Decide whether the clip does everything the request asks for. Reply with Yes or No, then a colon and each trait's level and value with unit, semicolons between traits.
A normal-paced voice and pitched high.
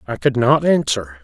No: average, 195 wpm; medium, 140 Hz